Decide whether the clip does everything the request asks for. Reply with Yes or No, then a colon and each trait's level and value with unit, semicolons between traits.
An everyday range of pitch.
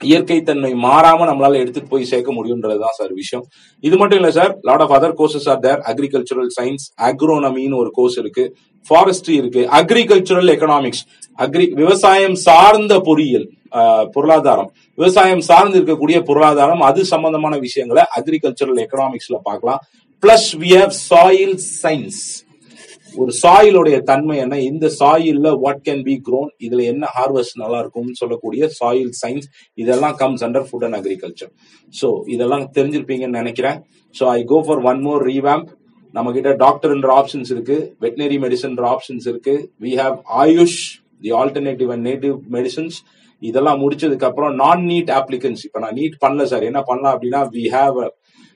Yes: average, 4.7 semitones